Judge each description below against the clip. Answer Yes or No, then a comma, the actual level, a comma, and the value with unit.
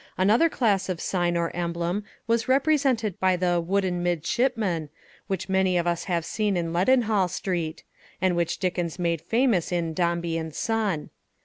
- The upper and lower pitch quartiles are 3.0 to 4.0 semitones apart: Yes, average, 3.7 semitones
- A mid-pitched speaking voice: Yes, medium, 180 Hz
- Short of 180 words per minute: Yes, average, 155 wpm